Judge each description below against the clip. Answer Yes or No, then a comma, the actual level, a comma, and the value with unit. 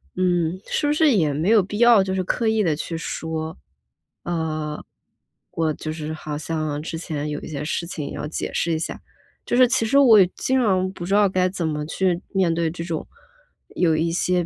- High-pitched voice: No, medium, 170 Hz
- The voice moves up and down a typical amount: Yes, average, 3.4 semitones